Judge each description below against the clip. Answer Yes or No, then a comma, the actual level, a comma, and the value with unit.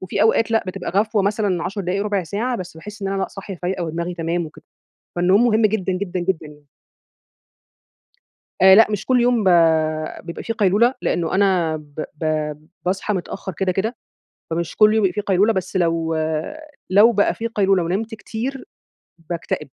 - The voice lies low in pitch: No, high, 195 Hz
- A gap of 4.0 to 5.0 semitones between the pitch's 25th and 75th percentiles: No, average, 3.4 semitones